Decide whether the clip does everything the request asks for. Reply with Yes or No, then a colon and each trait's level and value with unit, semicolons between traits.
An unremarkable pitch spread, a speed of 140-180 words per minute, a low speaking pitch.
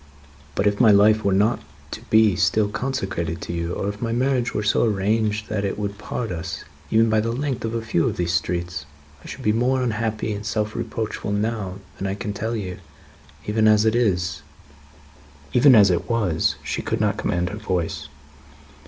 No: average, 3.6 semitones; fast, 205 wpm; low, 105 Hz